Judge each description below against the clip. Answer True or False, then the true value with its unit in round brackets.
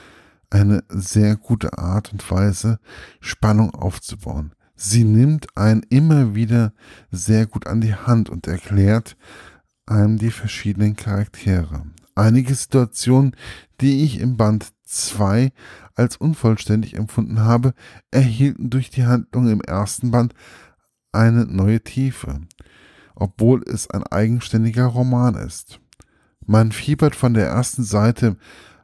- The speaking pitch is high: False (110 Hz)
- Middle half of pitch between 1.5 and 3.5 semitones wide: True (3.2 semitones)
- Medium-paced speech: False (120 wpm)